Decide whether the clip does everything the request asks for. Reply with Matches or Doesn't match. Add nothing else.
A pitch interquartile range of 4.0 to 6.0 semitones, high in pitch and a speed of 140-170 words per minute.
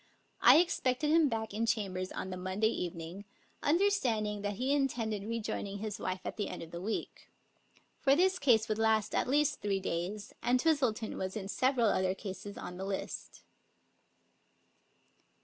Matches